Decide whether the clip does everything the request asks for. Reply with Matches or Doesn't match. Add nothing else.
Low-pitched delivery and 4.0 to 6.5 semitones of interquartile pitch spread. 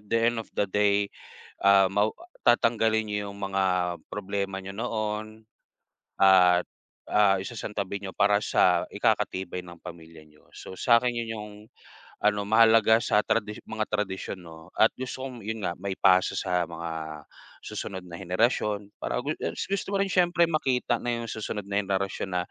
Doesn't match